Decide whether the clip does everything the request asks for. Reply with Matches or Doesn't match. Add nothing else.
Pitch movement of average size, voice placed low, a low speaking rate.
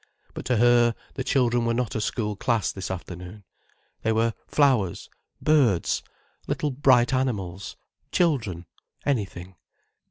Matches